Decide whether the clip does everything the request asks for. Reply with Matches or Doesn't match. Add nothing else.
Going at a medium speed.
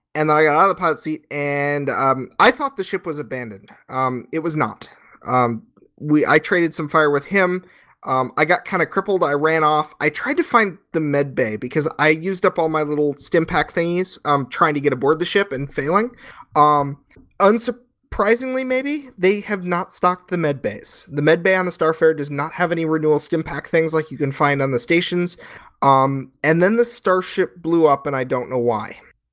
Doesn't match